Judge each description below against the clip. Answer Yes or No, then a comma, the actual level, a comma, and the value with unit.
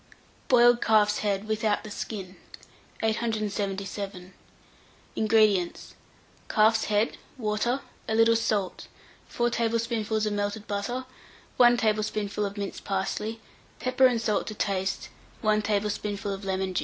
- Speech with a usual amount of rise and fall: No, narrow, 1.9 semitones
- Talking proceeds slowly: Yes, slow, 120 wpm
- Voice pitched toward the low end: No, high, 215 Hz